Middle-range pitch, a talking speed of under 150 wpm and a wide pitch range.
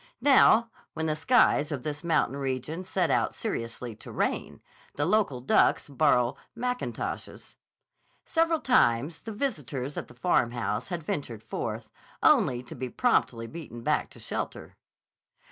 Yes: medium, 145 Hz; average, 140 wpm; wide, 7.0 semitones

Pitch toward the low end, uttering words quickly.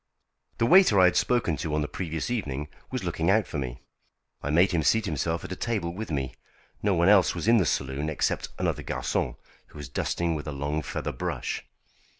Yes: very low, 85 Hz; fast, 210 wpm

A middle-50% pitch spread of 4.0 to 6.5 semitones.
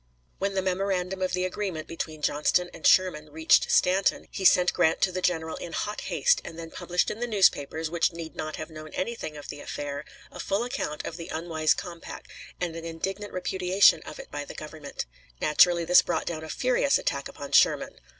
No: average, 3.0 semitones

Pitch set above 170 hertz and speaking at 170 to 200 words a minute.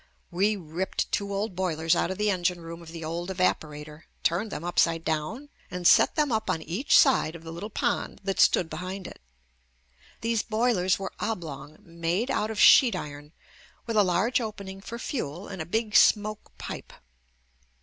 Yes: medium, 185 Hz; average, 180 wpm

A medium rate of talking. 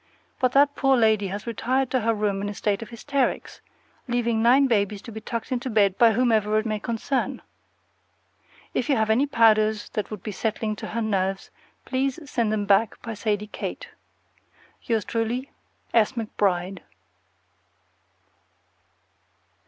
Yes: average, 150 wpm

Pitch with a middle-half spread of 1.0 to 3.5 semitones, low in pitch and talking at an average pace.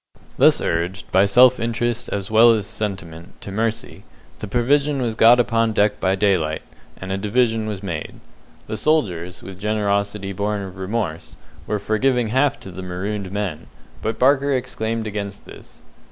Yes: average, 3.1 semitones; low, 105 Hz; average, 165 wpm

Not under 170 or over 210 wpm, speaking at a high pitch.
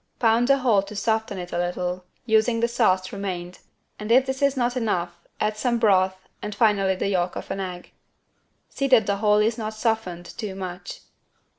Yes: average, 190 wpm; high, 210 Hz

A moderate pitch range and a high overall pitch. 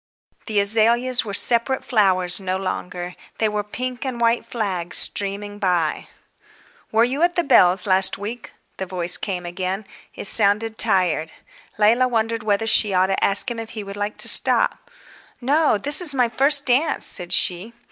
Yes: average, 4.2 semitones; high, 210 Hz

